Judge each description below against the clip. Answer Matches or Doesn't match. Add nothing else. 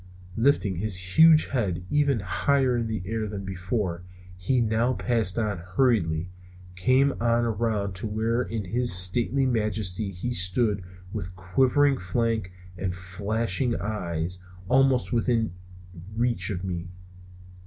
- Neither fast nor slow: Doesn't match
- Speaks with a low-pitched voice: Matches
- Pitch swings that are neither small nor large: Matches